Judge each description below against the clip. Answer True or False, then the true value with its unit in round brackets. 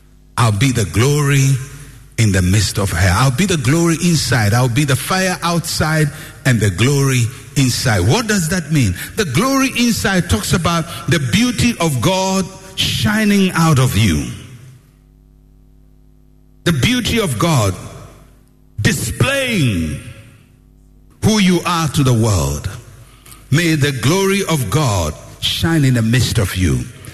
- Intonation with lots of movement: True (6.7 semitones)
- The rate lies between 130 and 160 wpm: True (135 wpm)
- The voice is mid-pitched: False (130 Hz)